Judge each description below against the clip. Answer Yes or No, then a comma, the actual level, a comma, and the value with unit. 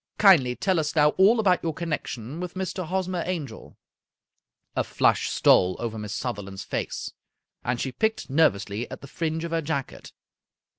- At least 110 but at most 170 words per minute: Yes, average, 160 wpm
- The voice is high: No, medium, 160 Hz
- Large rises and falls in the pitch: Yes, wide, 6.8 semitones